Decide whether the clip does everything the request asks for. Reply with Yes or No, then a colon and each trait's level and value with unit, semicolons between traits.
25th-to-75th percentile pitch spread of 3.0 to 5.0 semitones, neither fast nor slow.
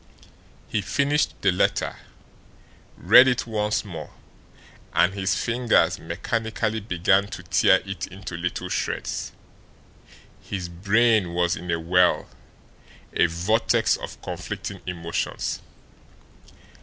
No: average, 4.1 semitones; slow, 105 wpm